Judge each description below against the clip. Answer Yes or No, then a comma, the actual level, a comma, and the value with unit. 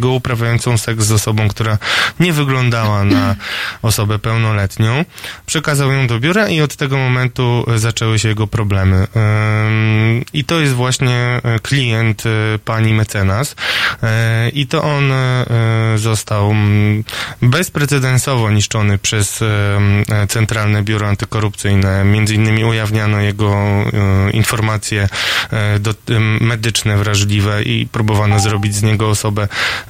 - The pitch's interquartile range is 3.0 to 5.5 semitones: No, narrow, 2.4 semitones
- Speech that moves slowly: Yes, slow, 105 wpm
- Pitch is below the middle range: Yes, low, 110 Hz